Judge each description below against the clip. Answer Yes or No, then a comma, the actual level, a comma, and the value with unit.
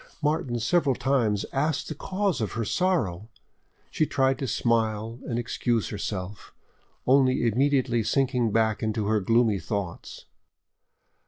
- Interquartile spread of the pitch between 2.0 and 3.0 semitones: No, average, 3.8 semitones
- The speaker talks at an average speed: No, slow, 130 wpm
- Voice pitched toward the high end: No, low, 120 Hz